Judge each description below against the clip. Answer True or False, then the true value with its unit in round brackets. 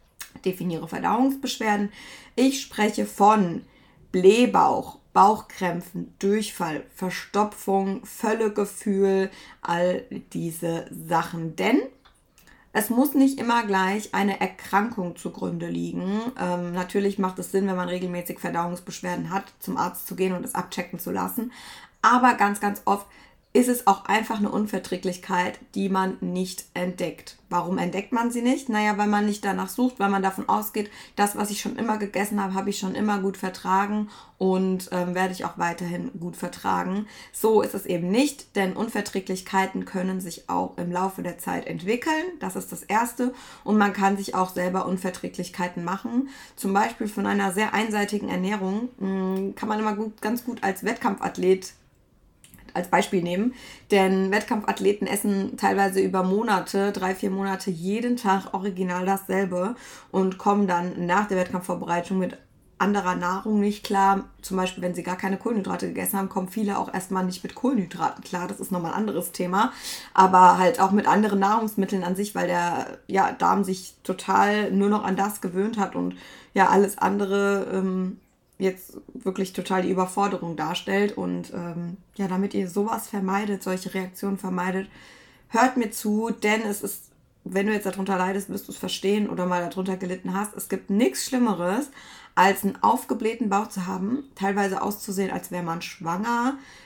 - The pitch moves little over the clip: True (2.2 semitones)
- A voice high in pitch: True (195 Hz)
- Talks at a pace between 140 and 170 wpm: True (160 wpm)